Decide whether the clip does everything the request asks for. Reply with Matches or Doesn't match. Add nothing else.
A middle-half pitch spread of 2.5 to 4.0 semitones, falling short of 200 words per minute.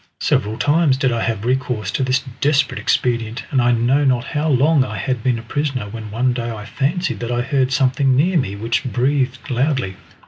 Doesn't match